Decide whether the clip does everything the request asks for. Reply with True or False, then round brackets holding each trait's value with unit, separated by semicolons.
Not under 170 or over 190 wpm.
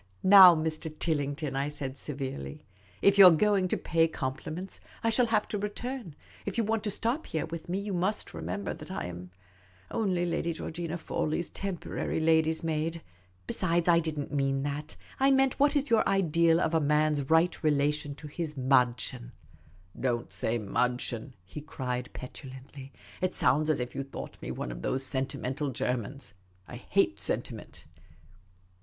True (180 wpm)